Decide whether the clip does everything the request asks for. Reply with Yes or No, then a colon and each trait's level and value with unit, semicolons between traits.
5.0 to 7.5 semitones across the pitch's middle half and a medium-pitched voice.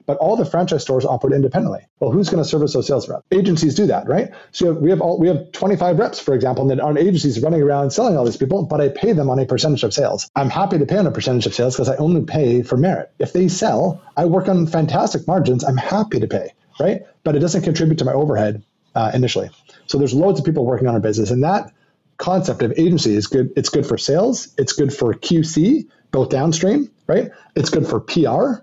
Yes: average, 5.3 semitones; medium, 155 Hz